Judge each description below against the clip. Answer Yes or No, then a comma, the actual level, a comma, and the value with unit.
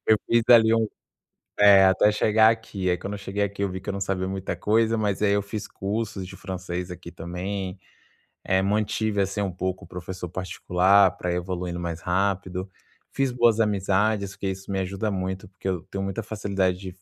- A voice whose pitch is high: No, very low, 95 Hz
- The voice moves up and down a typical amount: No, narrow, 2.0 semitones